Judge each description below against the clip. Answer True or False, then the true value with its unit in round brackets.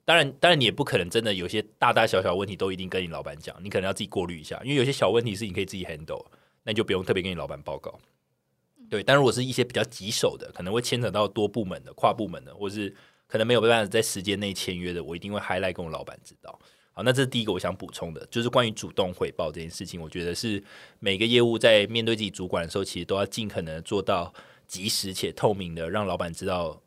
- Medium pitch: False (100 Hz)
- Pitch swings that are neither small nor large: True (4.0 semitones)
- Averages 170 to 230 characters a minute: False (420 characters per minute)